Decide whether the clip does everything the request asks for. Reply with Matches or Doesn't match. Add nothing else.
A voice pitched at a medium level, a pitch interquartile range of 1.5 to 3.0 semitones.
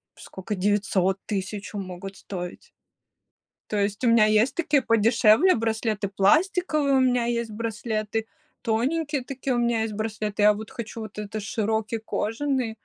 Doesn't match